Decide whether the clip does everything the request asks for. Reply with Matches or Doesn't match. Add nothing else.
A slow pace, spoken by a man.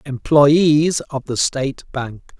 Matches